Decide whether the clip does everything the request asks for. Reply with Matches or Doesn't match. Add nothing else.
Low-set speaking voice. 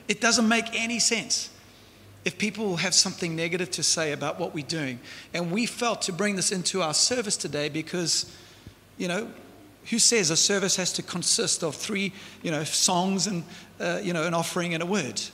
Doesn't match